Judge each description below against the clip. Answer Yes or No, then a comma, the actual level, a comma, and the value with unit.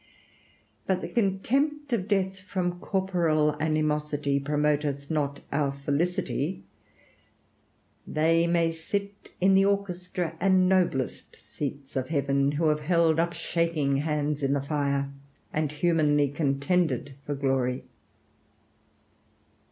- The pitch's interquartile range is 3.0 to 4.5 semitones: Yes, average, 4.2 semitones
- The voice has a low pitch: No, medium, 155 Hz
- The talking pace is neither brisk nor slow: No, slow, 115 wpm